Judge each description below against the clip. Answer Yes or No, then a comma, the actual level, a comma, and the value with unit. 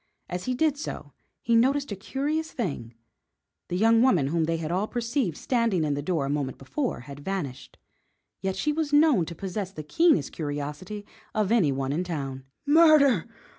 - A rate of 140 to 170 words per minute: No, average, 180 wpm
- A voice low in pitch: No, high, 190 Hz